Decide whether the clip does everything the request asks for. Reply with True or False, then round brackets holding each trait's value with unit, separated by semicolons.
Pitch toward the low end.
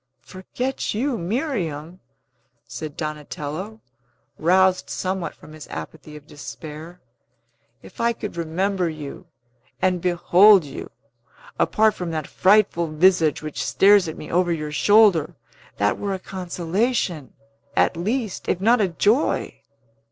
False (180 Hz)